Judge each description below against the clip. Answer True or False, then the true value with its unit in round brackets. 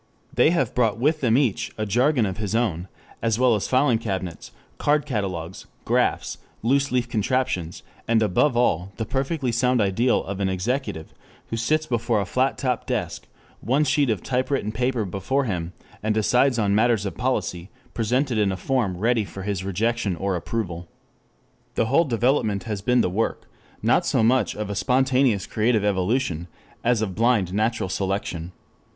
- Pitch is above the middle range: False (115 Hz)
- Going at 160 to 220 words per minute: True (170 wpm)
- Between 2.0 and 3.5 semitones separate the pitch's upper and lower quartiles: False (4.4 semitones)